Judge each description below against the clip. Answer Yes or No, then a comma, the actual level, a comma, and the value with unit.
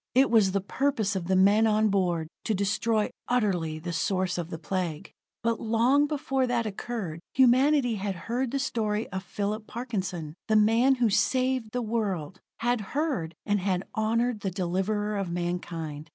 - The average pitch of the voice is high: Yes, high, 210 Hz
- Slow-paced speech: No, average, 165 wpm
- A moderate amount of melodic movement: Yes, average, 4.3 semitones